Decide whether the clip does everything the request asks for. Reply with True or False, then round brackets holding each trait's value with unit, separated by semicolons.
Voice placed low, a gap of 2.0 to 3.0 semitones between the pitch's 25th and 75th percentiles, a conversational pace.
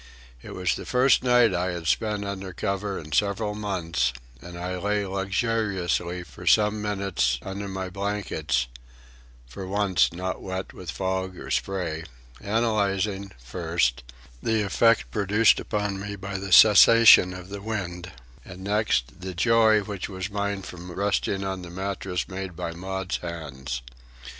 True (95 Hz; 2.5 semitones; 150 wpm)